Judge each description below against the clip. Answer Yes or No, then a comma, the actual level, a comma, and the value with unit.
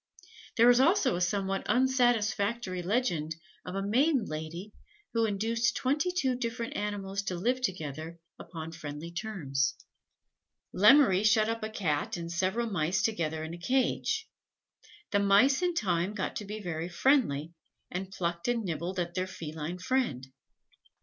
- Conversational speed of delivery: Yes, average, 150 wpm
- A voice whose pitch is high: Yes, high, 195 Hz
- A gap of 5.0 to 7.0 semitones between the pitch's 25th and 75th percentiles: Yes, wide, 5.4 semitones